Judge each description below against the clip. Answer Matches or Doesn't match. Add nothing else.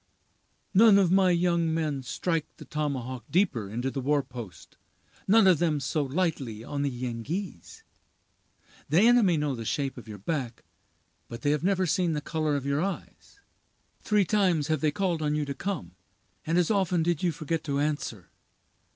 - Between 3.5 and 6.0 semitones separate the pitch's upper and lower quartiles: Matches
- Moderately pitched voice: Matches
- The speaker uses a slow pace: Doesn't match